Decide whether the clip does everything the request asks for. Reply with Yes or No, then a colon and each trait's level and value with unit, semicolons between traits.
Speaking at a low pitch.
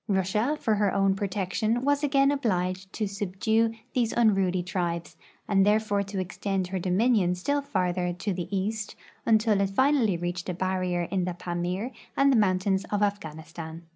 No: high, 195 Hz